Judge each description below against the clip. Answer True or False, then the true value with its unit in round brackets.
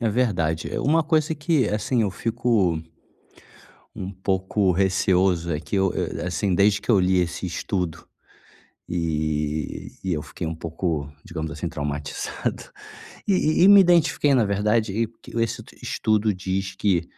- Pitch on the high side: False (95 Hz)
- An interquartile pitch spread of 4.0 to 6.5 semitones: True (5.1 semitones)